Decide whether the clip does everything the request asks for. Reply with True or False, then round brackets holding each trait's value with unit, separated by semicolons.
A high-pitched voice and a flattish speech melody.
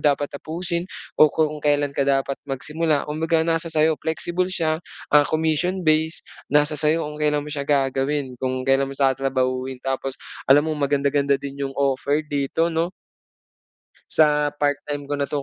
False (145 Hz; 2.3 semitones)